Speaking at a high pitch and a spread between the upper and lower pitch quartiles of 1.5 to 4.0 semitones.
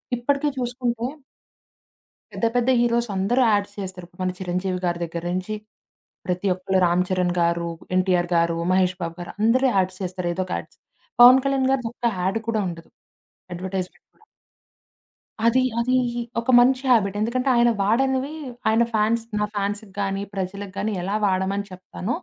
No: high, 200 Hz; average, 4.4 semitones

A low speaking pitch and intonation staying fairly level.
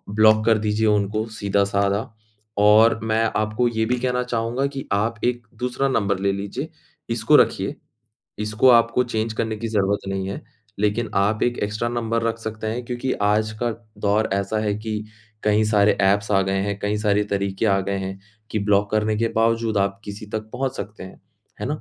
Yes: low, 110 Hz; narrow, 2.1 semitones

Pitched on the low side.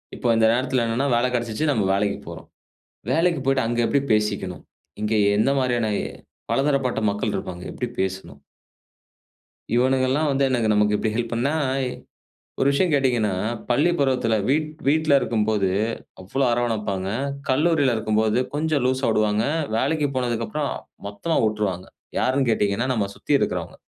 Yes: low, 120 Hz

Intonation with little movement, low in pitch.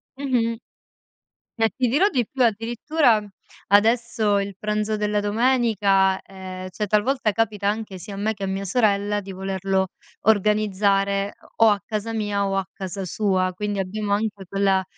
No: narrow, 2.3 semitones; high, 205 Hz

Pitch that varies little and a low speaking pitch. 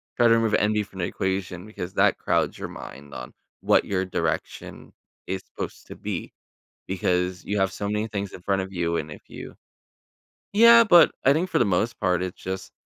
No: average, 3.1 semitones; very low, 95 Hz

